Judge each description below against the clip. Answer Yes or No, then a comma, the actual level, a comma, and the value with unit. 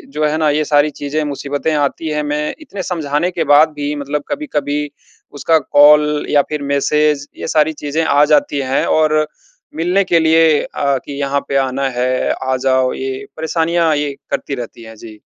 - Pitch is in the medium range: Yes, medium, 150 Hz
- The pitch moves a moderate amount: No, narrow, 2.1 semitones